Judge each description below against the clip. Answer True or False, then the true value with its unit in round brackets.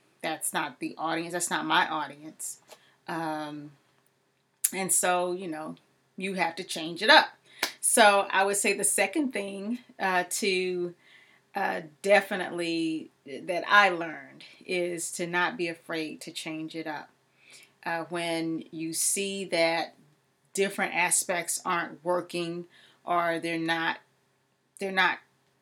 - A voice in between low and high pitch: True (175 Hz)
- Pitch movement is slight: False (3.4 semitones)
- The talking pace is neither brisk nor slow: False (130 wpm)